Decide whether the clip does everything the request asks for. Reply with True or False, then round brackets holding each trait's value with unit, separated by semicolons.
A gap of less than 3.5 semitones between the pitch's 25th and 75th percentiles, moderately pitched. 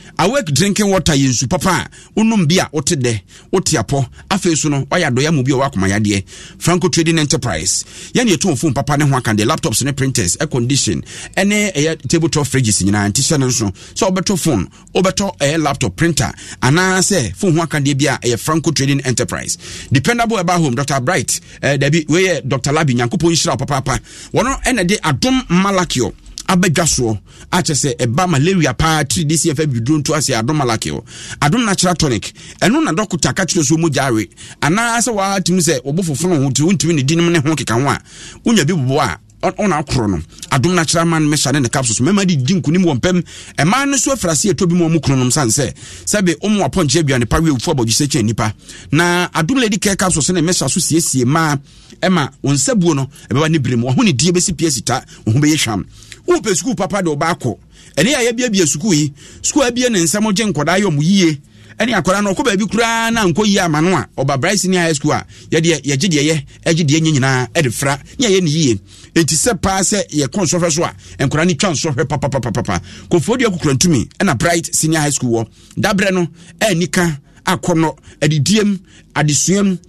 False (5.1 semitones; 160 Hz)